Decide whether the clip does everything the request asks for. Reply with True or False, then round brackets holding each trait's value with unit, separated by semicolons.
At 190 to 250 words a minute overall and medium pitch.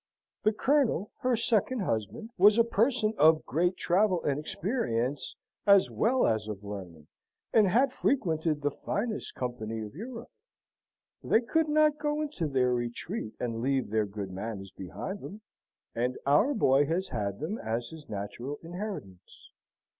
False (150 wpm; 160 Hz)